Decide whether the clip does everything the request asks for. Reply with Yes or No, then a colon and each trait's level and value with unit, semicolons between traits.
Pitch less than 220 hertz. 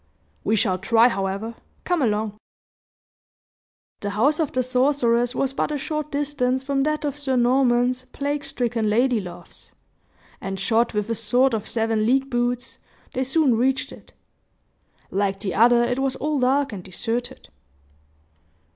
No: high, 245 Hz